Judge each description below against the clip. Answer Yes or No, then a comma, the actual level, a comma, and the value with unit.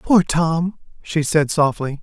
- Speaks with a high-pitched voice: No, medium, 160 Hz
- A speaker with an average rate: Yes, average, 150 wpm